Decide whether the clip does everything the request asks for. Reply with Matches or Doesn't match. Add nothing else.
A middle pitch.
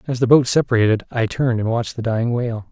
Doesn't match